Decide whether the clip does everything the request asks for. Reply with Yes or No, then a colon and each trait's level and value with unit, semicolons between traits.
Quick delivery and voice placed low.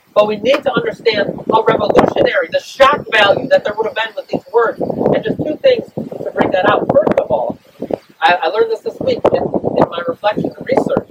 No: fast, 210 wpm; very high, 280 Hz